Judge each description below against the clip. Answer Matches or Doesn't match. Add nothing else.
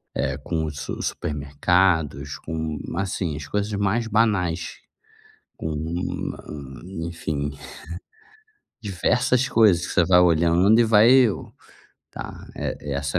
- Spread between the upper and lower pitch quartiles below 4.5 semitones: Doesn't match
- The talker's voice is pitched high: Doesn't match